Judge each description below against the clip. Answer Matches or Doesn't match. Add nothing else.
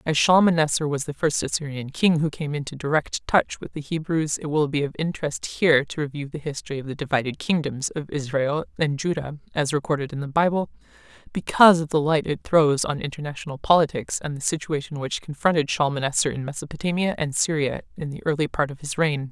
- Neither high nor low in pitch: Matches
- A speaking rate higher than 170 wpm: Matches